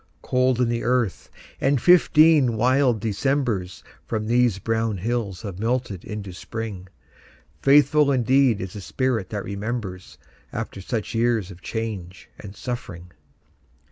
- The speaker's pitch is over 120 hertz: No, low, 115 Hz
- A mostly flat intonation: No, average, 4.3 semitones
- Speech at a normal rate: No, slow, 130 wpm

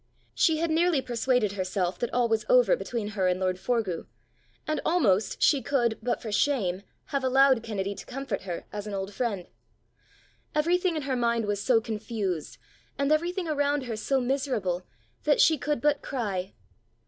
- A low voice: No, high, 240 Hz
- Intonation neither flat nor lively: No, wide, 6.0 semitones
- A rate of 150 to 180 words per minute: Yes, average, 170 wpm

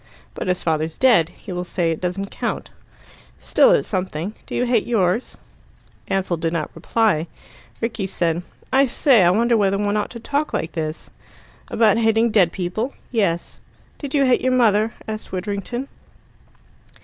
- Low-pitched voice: No, high, 205 Hz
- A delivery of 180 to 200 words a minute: No, average, 165 wpm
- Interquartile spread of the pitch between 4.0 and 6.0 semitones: Yes, average, 4.9 semitones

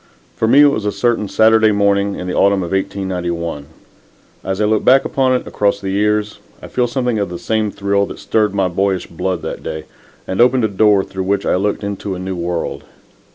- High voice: No, low, 100 Hz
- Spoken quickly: Yes, fast, 215 wpm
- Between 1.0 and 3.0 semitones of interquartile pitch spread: Yes, narrow, 2.6 semitones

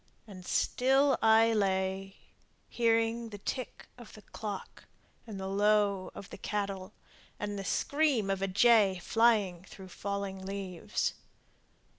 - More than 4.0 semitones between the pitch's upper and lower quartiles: No, average, 2.7 semitones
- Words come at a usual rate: No, slow, 125 wpm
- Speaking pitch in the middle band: No, high, 200 Hz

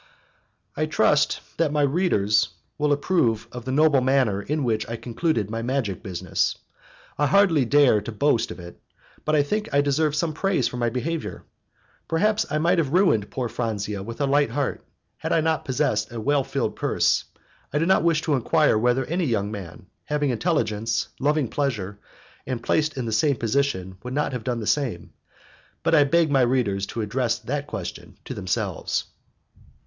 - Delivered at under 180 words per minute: No, average, 185 wpm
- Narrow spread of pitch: No, average, 5.3 semitones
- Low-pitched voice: Yes, low, 130 Hz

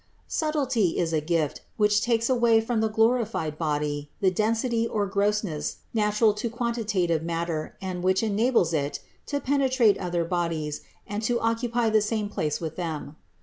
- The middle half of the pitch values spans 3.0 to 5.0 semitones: No, wide, 5.4 semitones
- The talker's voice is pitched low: No, high, 210 Hz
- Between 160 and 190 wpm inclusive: Yes, average, 165 wpm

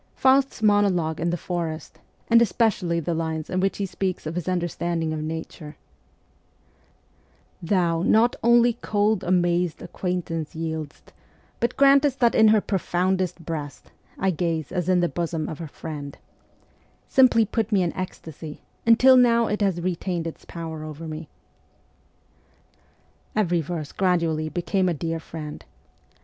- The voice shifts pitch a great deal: No, average, 4.1 semitones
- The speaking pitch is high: No, medium, 175 Hz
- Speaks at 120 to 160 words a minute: Yes, average, 145 wpm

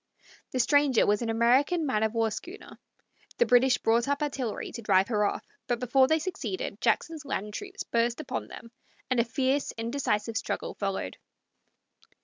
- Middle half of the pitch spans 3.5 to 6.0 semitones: Yes, average, 4.0 semitones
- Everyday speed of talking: Yes, average, 165 wpm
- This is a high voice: Yes, high, 245 Hz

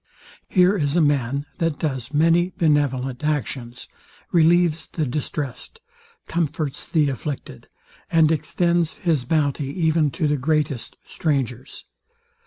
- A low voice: No, medium, 150 Hz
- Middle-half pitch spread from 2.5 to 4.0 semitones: Yes, average, 3.3 semitones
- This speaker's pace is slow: Yes, slow, 115 wpm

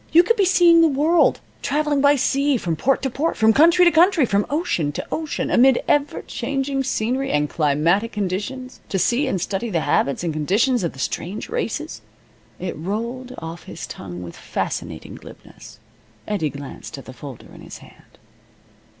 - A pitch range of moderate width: No, wide, 9.0 semitones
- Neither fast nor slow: Yes, average, 180 wpm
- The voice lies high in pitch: Yes, high, 240 Hz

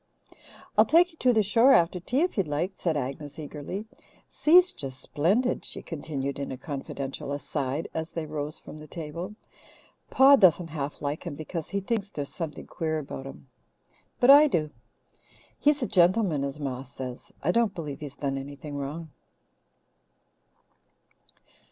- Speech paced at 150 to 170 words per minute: Yes, average, 160 wpm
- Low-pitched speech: No, medium, 155 Hz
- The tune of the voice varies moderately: No, wide, 5.7 semitones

